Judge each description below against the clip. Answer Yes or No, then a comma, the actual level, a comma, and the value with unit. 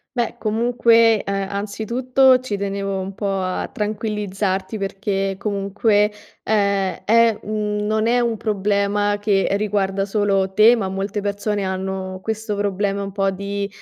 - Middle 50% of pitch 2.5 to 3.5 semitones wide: No, narrow, 1.6 semitones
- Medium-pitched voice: No, high, 205 Hz